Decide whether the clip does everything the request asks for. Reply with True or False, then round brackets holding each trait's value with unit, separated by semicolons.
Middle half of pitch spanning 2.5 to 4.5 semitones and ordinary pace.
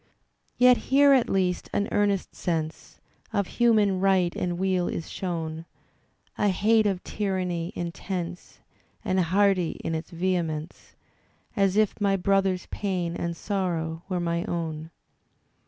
False (2.8 semitones; 130 wpm)